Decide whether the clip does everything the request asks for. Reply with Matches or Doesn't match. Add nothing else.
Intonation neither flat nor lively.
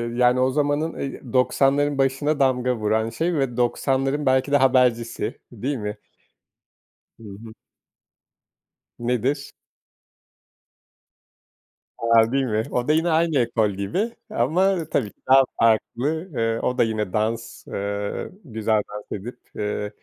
Matches